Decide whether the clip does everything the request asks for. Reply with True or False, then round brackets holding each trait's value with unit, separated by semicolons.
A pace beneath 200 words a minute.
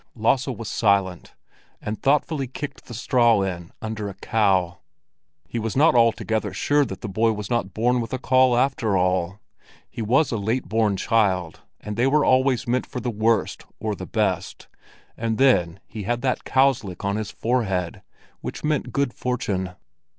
True (175 wpm)